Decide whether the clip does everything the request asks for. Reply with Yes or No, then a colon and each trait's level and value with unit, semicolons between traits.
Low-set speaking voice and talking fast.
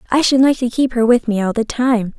No: high, 240 Hz; fast, 300 wpm